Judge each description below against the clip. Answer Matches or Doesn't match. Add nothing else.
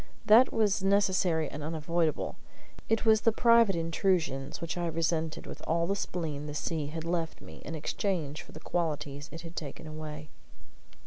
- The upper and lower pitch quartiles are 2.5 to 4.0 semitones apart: Matches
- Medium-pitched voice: Matches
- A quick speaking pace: Doesn't match